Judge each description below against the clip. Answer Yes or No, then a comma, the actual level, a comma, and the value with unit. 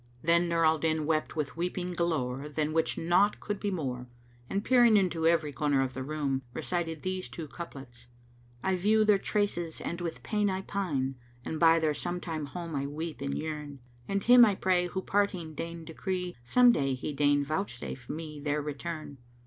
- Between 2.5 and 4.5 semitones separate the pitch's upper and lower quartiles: Yes, average, 4.0 semitones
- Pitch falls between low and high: Yes, medium, 165 Hz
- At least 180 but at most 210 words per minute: Yes, average, 190 wpm